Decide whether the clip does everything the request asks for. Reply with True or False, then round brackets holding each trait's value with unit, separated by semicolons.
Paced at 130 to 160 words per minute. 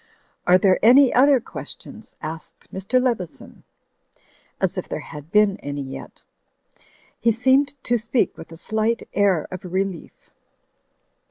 True (140 wpm)